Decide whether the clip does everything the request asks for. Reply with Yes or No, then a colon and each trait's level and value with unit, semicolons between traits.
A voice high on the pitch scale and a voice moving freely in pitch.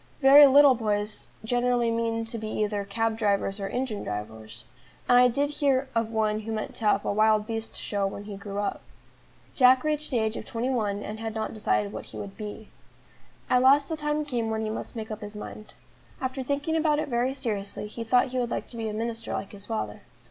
No: high, 225 Hz; average, 3.4 semitones